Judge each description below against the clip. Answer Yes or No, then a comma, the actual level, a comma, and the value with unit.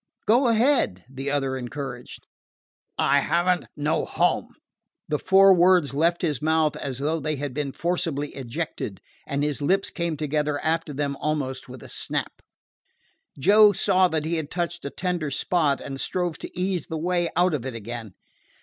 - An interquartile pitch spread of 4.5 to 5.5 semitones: No, average, 4.1 semitones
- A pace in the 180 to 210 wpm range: No, average, 170 wpm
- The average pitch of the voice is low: No, medium, 155 Hz